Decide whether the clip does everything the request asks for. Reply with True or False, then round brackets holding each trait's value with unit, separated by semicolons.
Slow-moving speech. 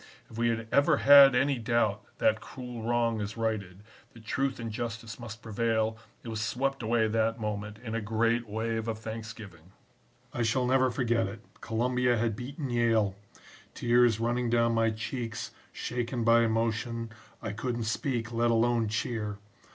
False (160 wpm)